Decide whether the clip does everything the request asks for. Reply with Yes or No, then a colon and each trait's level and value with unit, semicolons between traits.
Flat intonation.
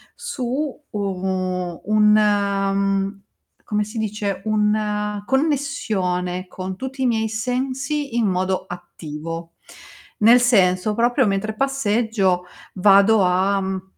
No: average, 4.0 semitones